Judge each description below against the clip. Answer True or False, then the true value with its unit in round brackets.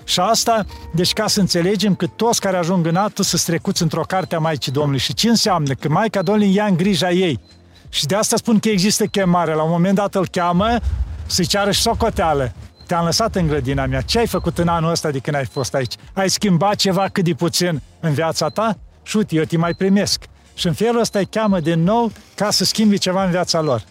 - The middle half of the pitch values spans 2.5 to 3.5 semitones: False (4.1 semitones)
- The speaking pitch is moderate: True (180 Hz)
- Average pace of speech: False (230 wpm)